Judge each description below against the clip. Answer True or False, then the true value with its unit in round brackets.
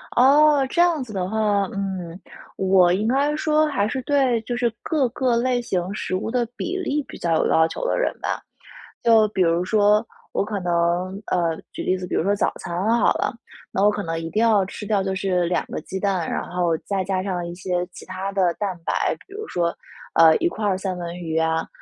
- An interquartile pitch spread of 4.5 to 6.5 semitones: True (4.9 semitones)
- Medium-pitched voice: False (195 Hz)